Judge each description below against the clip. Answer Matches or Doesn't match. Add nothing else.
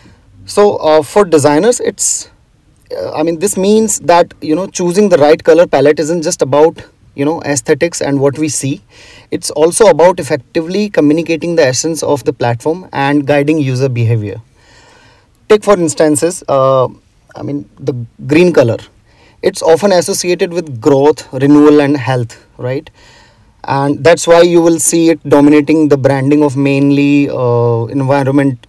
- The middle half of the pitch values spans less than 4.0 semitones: Matches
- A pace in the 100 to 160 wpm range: Matches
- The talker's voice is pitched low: Doesn't match